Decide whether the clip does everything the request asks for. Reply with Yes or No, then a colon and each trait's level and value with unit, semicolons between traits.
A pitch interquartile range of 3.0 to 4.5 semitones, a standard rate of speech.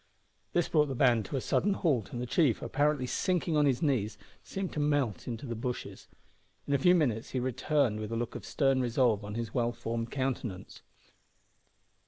Yes: average, 4.1 semitones; average, 195 wpm